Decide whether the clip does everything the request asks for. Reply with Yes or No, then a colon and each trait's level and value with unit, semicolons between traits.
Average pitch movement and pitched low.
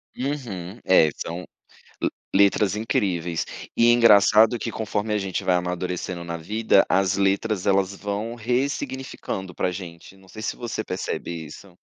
Yes: average, 3.5 semitones; low, 100 Hz